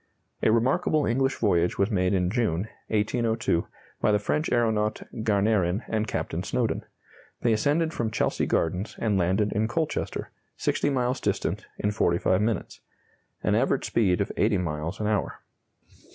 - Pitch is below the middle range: Yes, low, 105 Hz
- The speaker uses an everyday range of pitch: Yes, average, 3.5 semitones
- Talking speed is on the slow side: No, average, 150 wpm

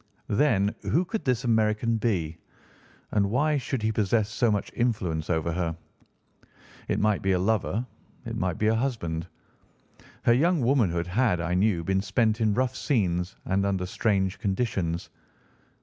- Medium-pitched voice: No, low, 105 Hz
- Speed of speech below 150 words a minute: No, average, 155 wpm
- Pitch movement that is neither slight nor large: Yes, average, 4.5 semitones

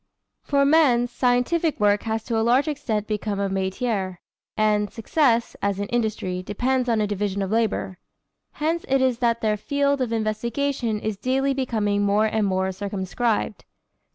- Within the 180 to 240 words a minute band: No, average, 160 wpm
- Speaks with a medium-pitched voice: No, high, 220 Hz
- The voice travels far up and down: No, average, 3.8 semitones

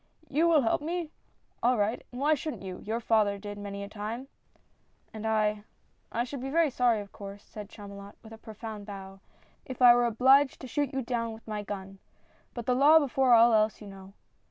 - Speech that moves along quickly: Yes, fast, 230 wpm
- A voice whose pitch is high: Yes, high, 225 Hz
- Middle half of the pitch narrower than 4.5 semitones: Yes, average, 4.0 semitones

